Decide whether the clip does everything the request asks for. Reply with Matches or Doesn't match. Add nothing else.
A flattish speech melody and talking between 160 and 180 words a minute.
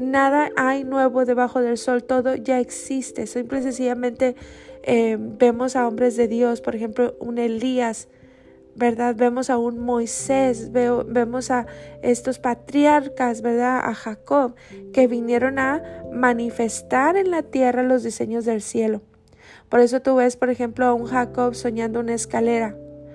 Doesn't match